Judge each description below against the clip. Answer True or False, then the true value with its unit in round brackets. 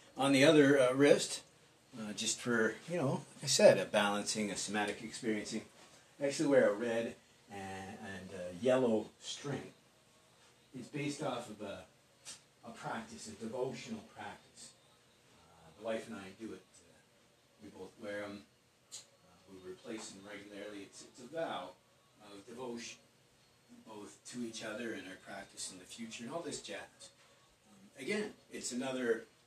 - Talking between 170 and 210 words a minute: False (160 wpm)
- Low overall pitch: True (110 Hz)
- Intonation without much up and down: False (3.5 semitones)